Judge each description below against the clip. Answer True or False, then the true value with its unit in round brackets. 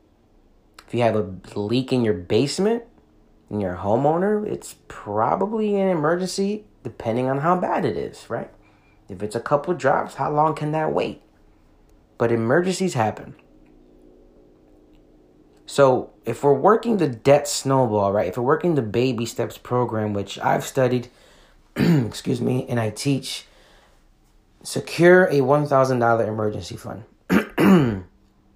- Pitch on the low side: True (120 Hz)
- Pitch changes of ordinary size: False (6.4 semitones)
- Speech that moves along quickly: False (140 wpm)